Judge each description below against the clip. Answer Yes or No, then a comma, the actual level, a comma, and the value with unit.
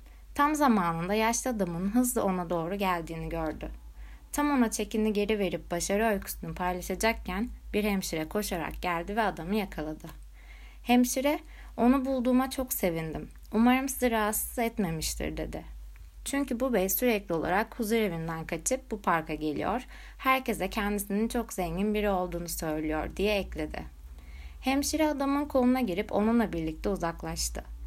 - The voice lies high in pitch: Yes, high, 200 Hz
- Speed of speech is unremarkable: Yes, average, 130 wpm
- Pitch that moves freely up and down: Yes, wide, 6.2 semitones